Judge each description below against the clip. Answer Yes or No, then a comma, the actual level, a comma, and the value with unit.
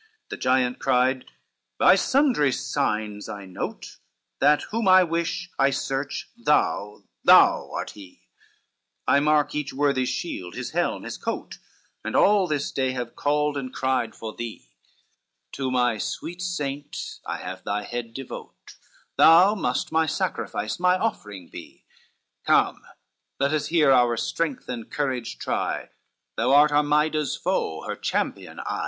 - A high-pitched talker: No, medium, 140 Hz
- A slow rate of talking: No, average, 145 wpm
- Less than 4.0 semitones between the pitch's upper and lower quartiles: No, average, 4.7 semitones